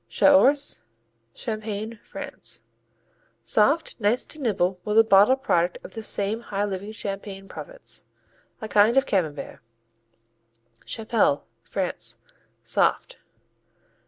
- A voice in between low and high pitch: No, high, 215 Hz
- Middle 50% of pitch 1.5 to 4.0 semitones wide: Yes, average, 3.0 semitones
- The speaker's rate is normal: No, slow, 105 wpm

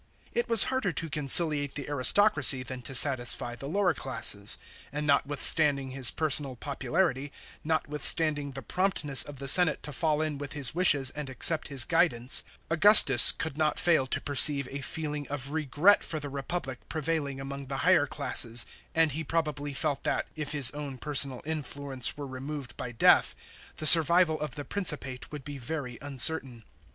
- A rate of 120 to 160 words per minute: No, average, 170 wpm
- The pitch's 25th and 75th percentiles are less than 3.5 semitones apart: Yes, average, 2.9 semitones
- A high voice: No, medium, 145 Hz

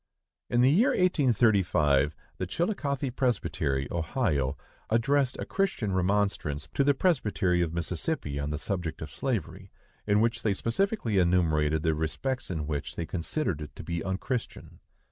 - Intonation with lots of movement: Yes, wide, 8.2 semitones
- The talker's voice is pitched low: Yes, very low, 95 Hz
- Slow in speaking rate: No, average, 145 wpm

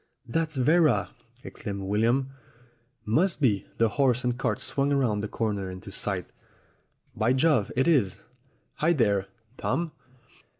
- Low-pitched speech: Yes, low, 120 Hz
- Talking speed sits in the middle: No, slow, 130 wpm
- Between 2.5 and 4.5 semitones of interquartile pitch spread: No, wide, 5.5 semitones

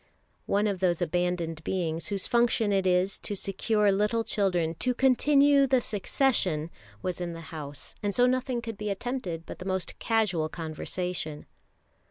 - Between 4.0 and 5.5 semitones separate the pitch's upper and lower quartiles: Yes, average, 4.8 semitones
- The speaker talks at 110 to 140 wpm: No, average, 160 wpm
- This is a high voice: Yes, high, 195 Hz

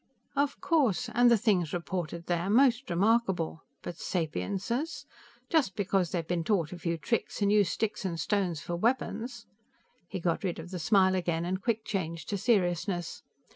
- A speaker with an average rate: Yes, average, 175 wpm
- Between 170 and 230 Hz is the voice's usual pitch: Yes, high, 190 Hz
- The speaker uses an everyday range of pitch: Yes, average, 4.6 semitones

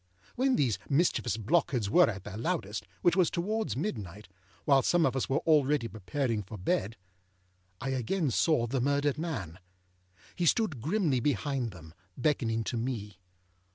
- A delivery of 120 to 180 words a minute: Yes, average, 155 wpm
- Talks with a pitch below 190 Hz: Yes, low, 135 Hz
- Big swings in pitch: Yes, wide, 6.1 semitones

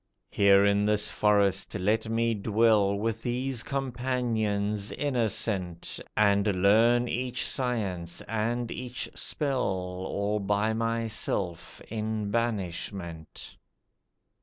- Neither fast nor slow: No, slow, 95 wpm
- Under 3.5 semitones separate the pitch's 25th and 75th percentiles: Yes, average, 2.7 semitones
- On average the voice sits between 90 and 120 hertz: Yes, low, 105 Hz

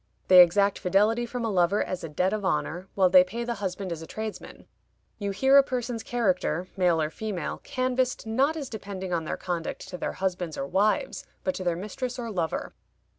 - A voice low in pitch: No, high, 195 Hz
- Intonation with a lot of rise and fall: No, average, 4.5 semitones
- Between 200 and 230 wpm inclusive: Yes, fast, 205 wpm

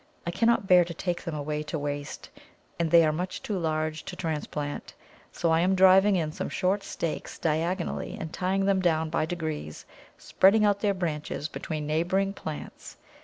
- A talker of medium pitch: Yes, medium, 170 Hz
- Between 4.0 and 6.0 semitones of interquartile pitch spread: No, average, 3.3 semitones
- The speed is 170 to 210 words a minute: Yes, average, 175 wpm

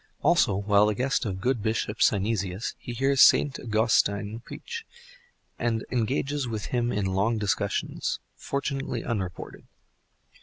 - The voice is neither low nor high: No, low, 110 Hz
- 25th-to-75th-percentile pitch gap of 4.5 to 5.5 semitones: No, average, 3.6 semitones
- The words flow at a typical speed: No, slow, 125 wpm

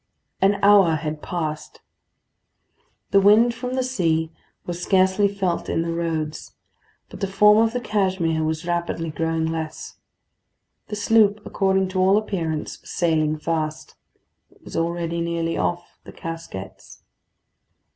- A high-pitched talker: No, medium, 170 Hz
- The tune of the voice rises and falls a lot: No, average, 3.6 semitones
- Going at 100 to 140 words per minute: Yes, slow, 135 wpm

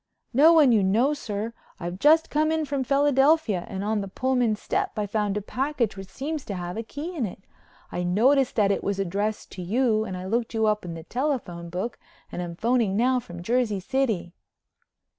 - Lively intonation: Yes, wide, 5.7 semitones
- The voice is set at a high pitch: Yes, high, 220 Hz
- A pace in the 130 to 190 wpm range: No, fast, 205 wpm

